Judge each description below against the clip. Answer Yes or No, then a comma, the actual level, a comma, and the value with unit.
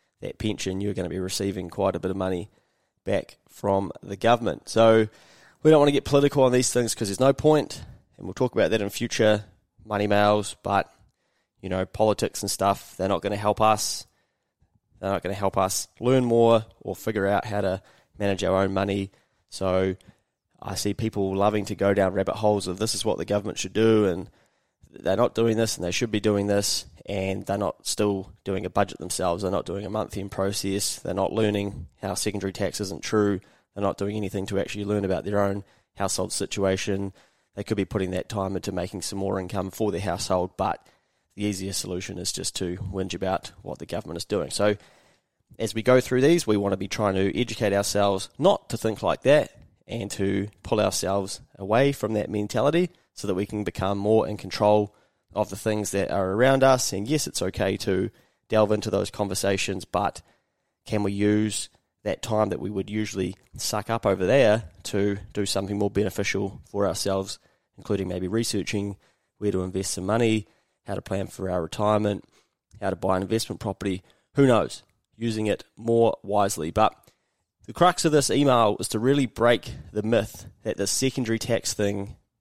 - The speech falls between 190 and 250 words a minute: Yes, average, 200 wpm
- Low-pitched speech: Yes, low, 100 Hz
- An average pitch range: No, narrow, 2.2 semitones